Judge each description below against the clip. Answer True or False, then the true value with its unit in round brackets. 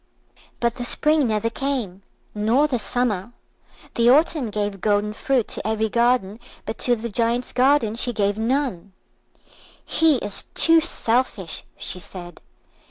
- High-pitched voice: True (230 Hz)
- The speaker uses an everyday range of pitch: True (3.7 semitones)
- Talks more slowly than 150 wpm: True (140 wpm)